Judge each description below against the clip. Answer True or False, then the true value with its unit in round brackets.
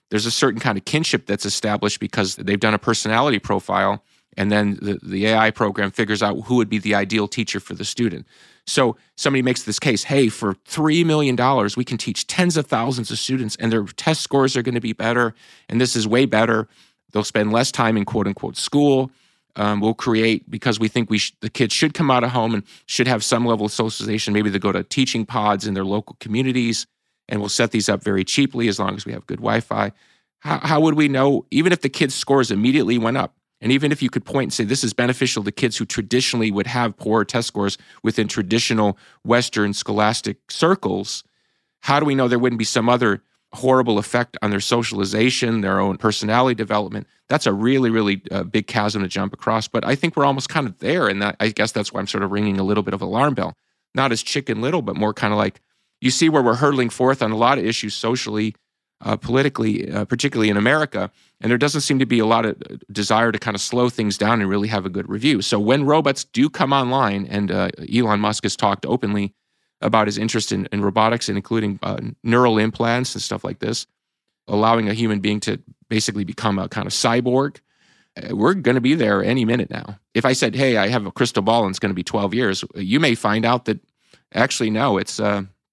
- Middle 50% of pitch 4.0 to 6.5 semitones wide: False (3.1 semitones)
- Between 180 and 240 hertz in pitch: False (110 Hz)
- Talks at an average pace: False (230 wpm)